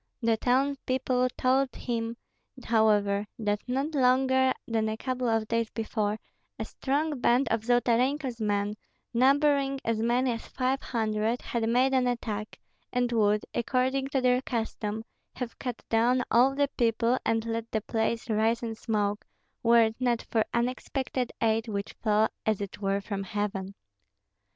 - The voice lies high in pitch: Yes, high, 235 Hz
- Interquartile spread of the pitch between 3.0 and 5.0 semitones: No, narrow, 2.6 semitones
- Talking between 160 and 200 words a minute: No, average, 150 wpm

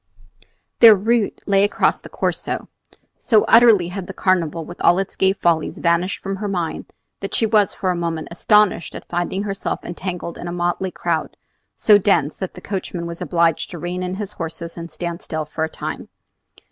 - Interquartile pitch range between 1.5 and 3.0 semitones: Yes, narrow, 2.6 semitones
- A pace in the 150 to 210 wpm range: Yes, average, 190 wpm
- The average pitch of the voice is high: No, medium, 180 Hz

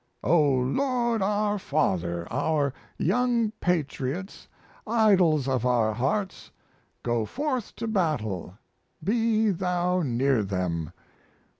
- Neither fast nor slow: No, slow, 100 wpm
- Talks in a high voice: No, medium, 160 Hz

